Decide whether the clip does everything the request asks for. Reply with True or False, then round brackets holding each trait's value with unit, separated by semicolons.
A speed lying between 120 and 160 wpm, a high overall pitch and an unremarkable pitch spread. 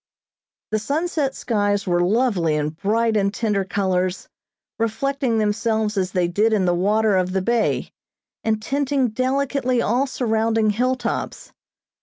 True (135 wpm; 220 Hz; 4.0 semitones)